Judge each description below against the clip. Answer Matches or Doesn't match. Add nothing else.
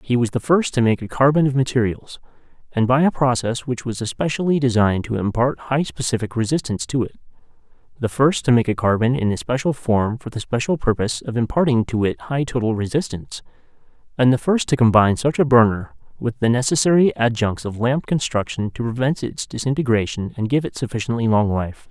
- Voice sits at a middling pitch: Doesn't match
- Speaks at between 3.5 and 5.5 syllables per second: Doesn't match